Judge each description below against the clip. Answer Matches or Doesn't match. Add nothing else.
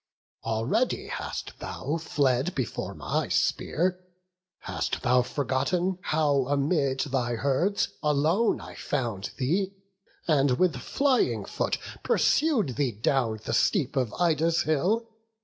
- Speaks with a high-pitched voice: Doesn't match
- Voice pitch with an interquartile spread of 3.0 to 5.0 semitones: Doesn't match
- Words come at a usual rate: Doesn't match